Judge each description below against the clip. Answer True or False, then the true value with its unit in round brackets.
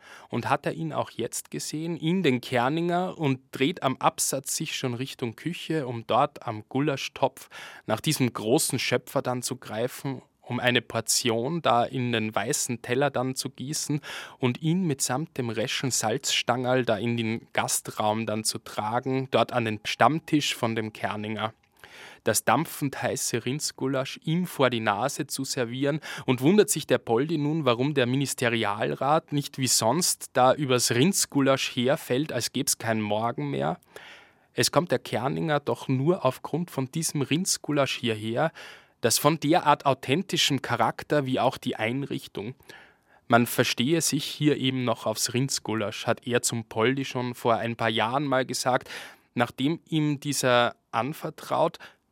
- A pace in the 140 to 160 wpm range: True (155 wpm)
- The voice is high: False (130 Hz)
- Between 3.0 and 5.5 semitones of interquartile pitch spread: True (3.6 semitones)